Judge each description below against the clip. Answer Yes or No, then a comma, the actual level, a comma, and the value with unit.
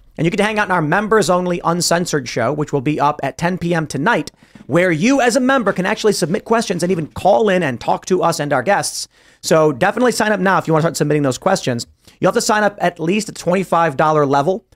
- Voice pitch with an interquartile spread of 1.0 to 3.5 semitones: No, average, 4.5 semitones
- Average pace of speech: No, fast, 250 wpm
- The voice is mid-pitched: Yes, medium, 175 Hz